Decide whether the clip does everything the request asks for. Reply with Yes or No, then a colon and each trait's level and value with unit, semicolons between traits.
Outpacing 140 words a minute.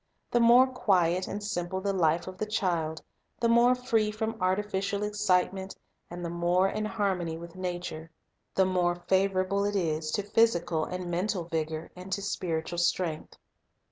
Yes: average, 170 wpm